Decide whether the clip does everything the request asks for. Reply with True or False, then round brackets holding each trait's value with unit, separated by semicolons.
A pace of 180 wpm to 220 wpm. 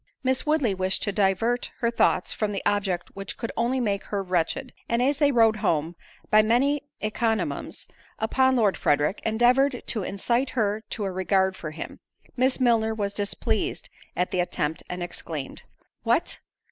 False (165 wpm)